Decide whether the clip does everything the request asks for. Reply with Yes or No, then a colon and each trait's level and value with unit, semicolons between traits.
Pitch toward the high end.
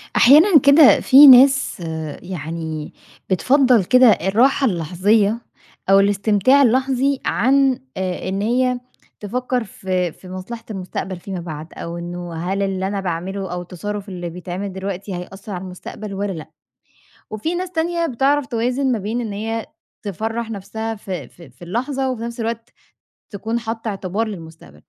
Yes: high, 205 Hz